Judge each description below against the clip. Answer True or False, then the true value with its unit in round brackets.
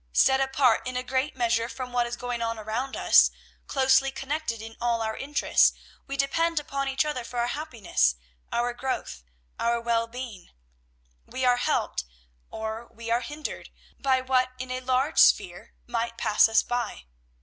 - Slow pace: False (170 wpm)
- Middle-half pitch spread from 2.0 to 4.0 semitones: True (2.5 semitones)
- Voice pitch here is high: True (245 Hz)